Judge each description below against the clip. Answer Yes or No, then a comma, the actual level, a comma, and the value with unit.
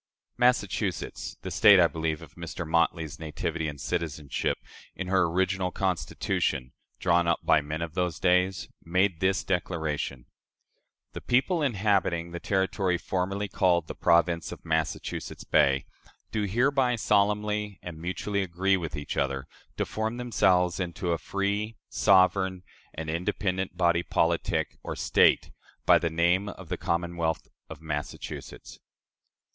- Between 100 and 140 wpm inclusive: Yes, slow, 135 wpm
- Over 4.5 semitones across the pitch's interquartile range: No, average, 3.0 semitones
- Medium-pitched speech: No, very low, 90 Hz